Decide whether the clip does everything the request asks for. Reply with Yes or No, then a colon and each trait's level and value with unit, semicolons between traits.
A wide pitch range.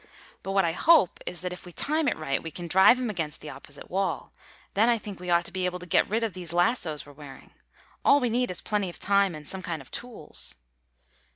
No: average, 4.4 semitones